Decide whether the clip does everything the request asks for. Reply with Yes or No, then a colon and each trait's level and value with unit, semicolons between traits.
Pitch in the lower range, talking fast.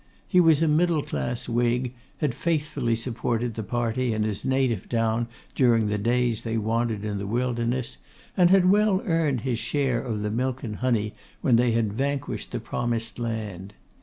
No: low, 120 Hz; average, 175 wpm